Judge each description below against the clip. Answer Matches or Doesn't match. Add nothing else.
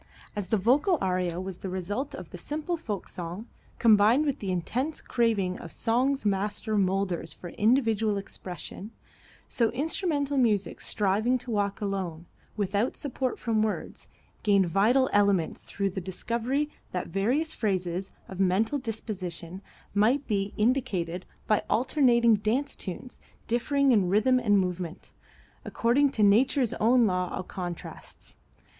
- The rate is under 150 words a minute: Matches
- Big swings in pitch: Doesn't match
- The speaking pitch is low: Doesn't match